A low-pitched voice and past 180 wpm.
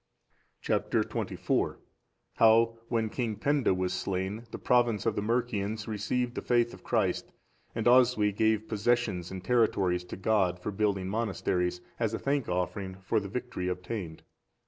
No: low, 110 Hz; average, 150 wpm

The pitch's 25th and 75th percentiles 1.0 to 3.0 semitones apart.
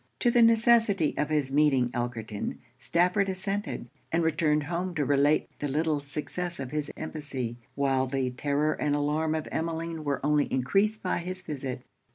No: average, 3.8 semitones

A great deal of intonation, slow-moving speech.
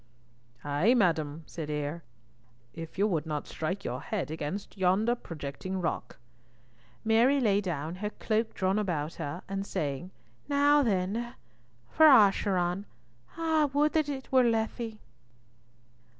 Yes: wide, 6.4 semitones; slow, 130 wpm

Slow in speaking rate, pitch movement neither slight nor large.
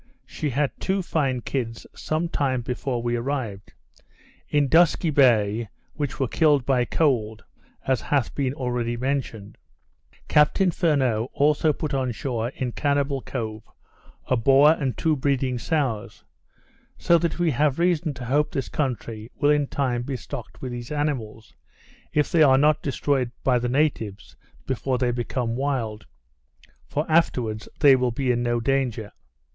No: average, 150 wpm; average, 3.6 semitones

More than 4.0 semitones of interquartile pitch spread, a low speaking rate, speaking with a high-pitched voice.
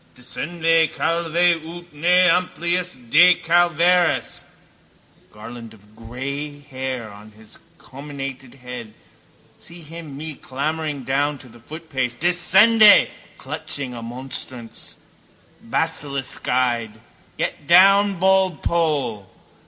No: wide, 5.5 semitones; slow, 95 wpm; medium, 145 Hz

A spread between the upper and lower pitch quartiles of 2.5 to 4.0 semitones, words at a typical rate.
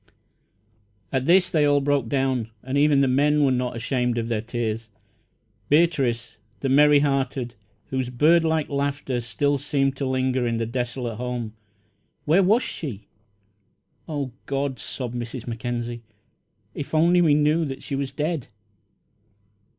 Yes: average, 3.3 semitones; average, 145 wpm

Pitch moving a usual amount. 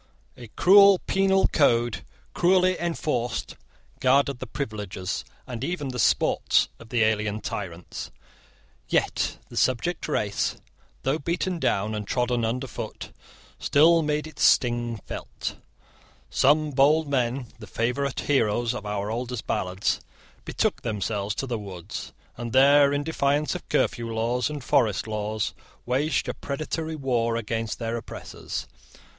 Yes: average, 4.7 semitones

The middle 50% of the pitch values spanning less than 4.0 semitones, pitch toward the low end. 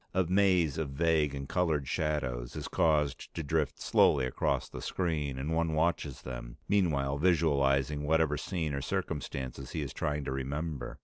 Yes: average, 3.1 semitones; very low, 75 Hz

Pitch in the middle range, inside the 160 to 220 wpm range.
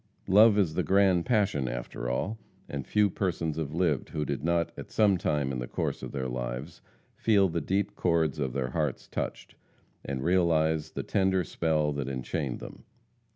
No: very low, 80 Hz; average, 180 wpm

